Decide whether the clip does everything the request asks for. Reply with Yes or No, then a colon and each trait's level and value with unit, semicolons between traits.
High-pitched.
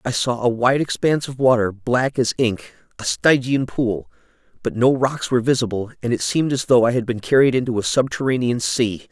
No: low, 125 Hz